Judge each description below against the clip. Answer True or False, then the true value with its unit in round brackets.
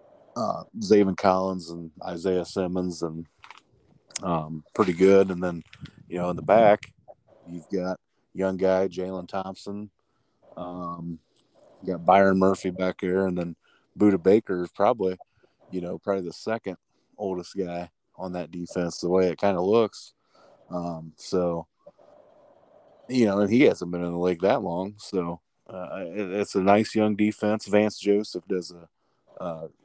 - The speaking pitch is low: True (95 Hz)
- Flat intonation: True (2.1 semitones)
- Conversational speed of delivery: True (155 wpm)